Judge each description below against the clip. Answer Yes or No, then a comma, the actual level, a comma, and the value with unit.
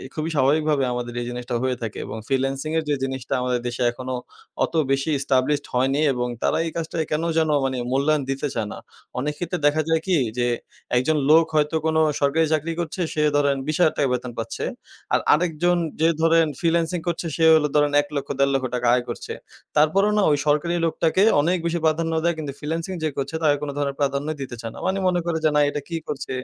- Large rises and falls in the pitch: No, average, 3.3 semitones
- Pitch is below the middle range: No, medium, 150 Hz